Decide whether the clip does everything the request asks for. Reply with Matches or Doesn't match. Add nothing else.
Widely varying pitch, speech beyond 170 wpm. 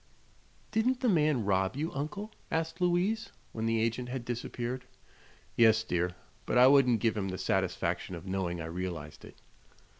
Doesn't match